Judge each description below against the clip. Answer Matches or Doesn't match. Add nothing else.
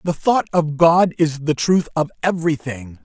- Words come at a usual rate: Matches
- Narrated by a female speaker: Doesn't match